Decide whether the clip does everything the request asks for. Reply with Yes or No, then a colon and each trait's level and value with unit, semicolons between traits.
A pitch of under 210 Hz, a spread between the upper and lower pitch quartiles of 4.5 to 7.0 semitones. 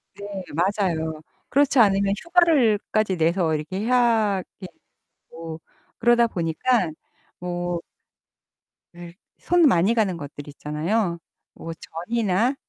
Yes: high, 190 Hz; wide, 5.5 semitones